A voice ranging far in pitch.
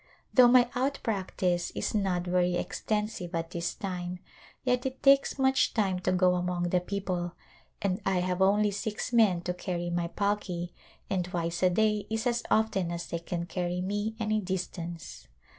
No: average, 3.2 semitones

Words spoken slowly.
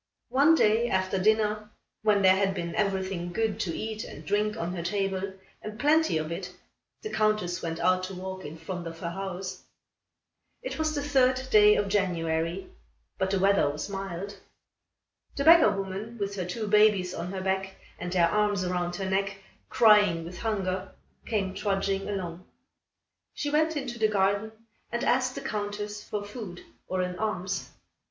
No: average, 170 wpm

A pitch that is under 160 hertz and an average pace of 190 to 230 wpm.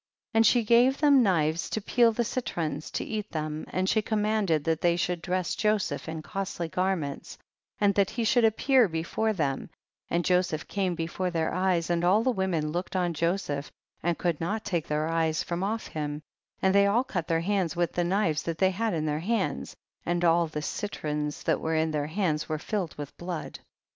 No: medium, 175 Hz; fast, 205 wpm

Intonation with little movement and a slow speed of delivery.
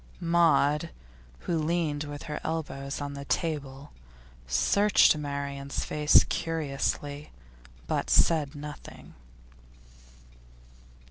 Yes: narrow, 2.2 semitones; slow, 85 wpm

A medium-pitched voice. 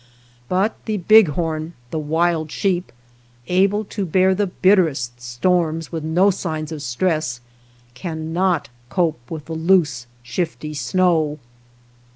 Yes: medium, 165 Hz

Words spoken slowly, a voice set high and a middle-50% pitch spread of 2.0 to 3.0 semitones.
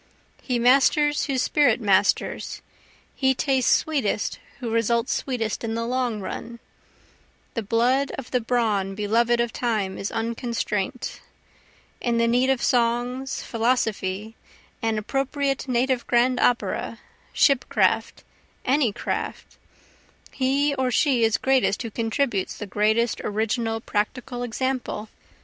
Yes: slow, 120 wpm; high, 240 Hz; average, 2.7 semitones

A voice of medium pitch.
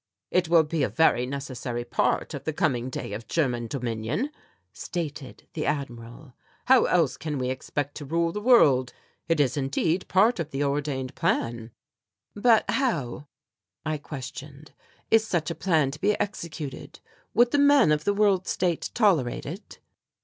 Yes: medium, 150 Hz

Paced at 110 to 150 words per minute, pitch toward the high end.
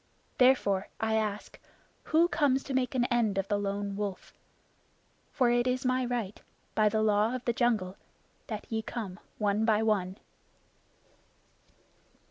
Yes: average, 145 wpm; high, 220 Hz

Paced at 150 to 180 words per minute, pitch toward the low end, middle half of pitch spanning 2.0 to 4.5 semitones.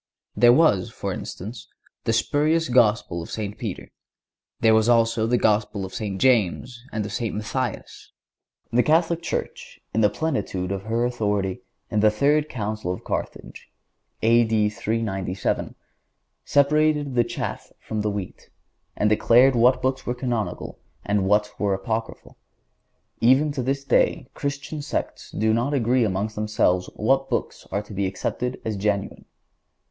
Yes: average, 155 wpm; low, 115 Hz; average, 3.6 semitones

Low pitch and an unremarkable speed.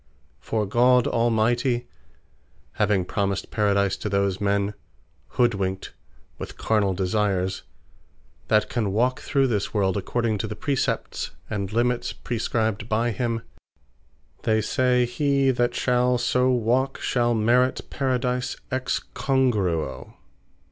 No: low, 115 Hz; slow, 115 wpm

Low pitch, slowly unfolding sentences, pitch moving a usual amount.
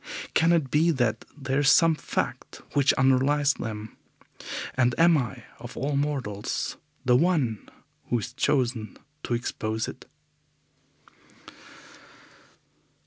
Yes: low, 130 Hz; slow, 115 wpm; average, 3.8 semitones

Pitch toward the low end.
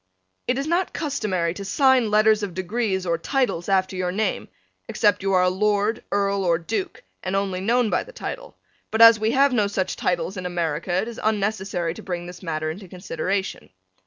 No: high, 195 Hz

